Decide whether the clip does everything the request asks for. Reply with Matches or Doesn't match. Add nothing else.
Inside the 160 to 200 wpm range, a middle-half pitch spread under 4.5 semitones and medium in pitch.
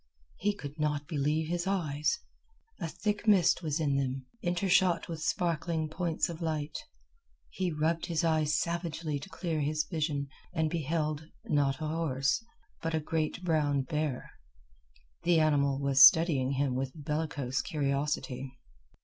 Doesn't match